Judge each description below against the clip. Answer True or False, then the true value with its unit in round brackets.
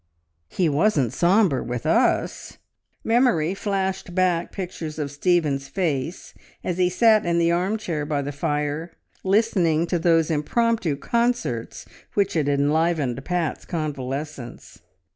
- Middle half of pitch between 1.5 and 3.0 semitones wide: False (4.3 semitones)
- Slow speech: True (125 wpm)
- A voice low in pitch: False (165 Hz)